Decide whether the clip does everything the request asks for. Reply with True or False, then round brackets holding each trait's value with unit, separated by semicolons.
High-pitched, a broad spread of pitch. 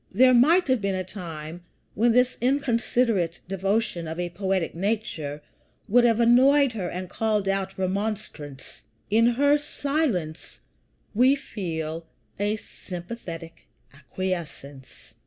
True (200 Hz; 5.7 semitones)